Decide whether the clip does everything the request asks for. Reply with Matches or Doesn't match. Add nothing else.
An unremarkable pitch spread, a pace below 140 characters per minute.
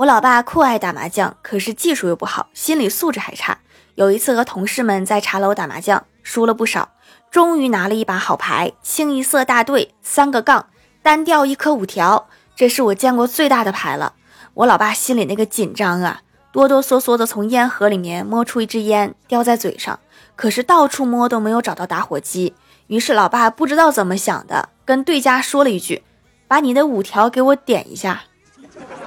Doesn't match